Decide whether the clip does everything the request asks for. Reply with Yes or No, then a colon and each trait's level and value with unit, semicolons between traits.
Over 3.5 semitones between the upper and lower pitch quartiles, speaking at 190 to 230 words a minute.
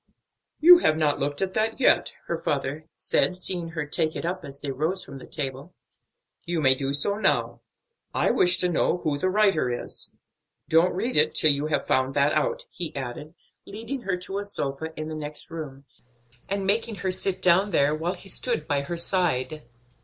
Yes: average, 4.7 semitones; average, 200 wpm